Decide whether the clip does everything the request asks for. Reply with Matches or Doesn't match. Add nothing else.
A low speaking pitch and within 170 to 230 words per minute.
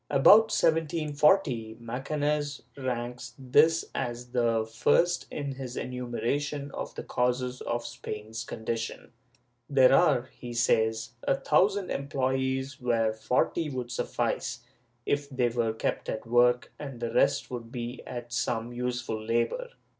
Doesn't match